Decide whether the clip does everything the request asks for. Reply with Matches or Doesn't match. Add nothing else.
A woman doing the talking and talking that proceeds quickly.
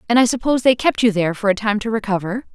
Matches